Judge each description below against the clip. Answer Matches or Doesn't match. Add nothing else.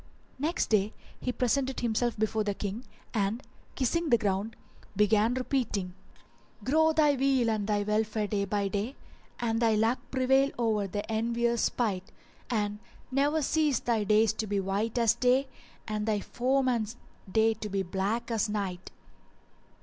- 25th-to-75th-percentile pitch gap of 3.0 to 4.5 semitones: Matches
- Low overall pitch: Doesn't match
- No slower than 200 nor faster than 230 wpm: Doesn't match